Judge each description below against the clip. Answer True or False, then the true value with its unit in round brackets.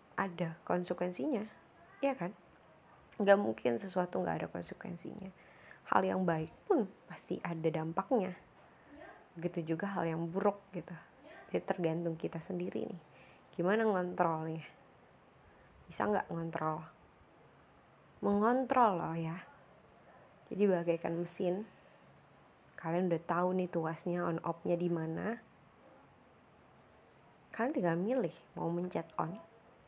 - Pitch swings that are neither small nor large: True (3.0 semitones)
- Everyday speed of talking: True (105 wpm)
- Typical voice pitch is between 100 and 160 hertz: False (175 Hz)